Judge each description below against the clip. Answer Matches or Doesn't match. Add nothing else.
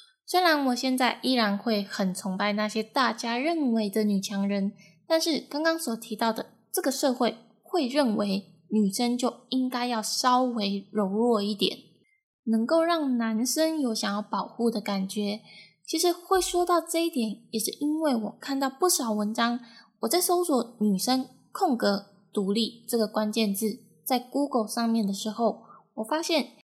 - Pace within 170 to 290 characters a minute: Matches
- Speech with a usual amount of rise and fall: Matches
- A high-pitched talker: Matches